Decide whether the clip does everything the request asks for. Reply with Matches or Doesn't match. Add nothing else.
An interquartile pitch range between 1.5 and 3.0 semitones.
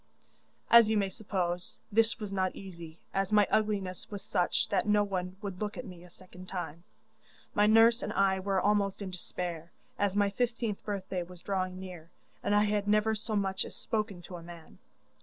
Matches